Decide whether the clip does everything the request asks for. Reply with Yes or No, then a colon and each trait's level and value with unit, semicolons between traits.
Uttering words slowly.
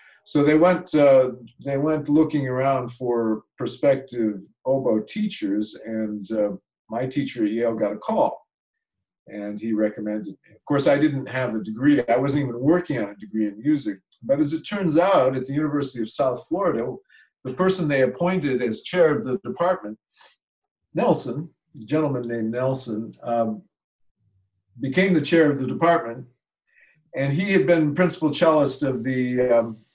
No: average, 165 wpm